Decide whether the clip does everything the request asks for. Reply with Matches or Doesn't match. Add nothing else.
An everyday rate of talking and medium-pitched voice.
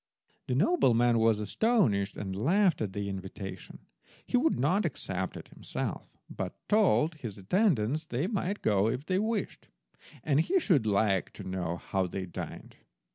Doesn't match